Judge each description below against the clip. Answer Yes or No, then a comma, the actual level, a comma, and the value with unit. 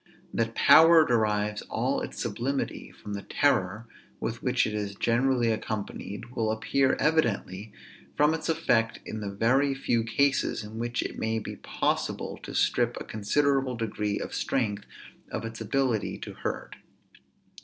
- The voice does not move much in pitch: No, average, 4.0 semitones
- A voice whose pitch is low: Yes, low, 115 Hz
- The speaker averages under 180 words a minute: Yes, average, 150 wpm